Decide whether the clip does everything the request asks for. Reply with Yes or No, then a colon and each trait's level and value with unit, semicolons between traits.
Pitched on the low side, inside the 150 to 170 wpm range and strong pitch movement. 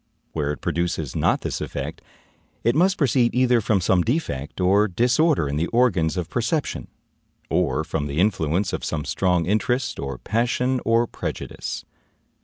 Yes: low, 100 Hz; average, 155 wpm; wide, 7.2 semitones